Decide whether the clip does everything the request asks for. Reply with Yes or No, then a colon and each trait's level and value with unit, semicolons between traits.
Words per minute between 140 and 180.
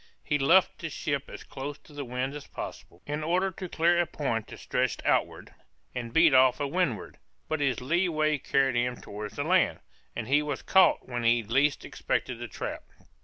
No: average, 200 wpm